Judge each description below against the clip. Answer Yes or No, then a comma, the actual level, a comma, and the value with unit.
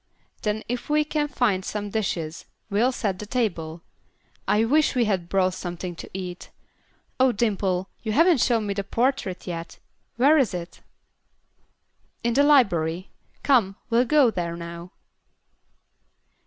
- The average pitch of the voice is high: Yes, high, 210 Hz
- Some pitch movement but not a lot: No, wide, 5.7 semitones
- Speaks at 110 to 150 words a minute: Yes, average, 140 wpm